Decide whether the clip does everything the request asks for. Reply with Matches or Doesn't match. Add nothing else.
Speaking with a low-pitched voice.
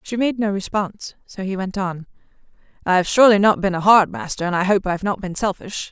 Doesn't match